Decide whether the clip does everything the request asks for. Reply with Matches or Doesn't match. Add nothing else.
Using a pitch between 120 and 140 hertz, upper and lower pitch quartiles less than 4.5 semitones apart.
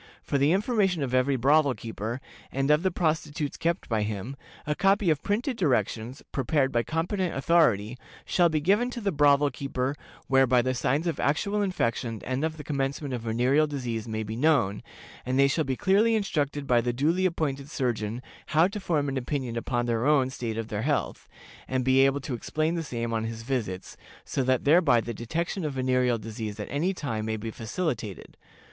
Doesn't match